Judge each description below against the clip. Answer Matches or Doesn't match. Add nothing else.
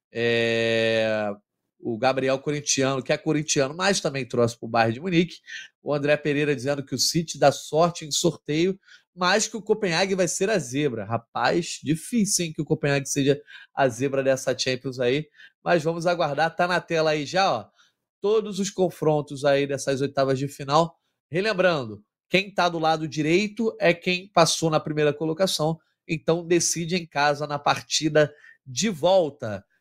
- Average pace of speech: Matches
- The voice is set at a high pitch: Doesn't match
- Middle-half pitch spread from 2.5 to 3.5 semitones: Doesn't match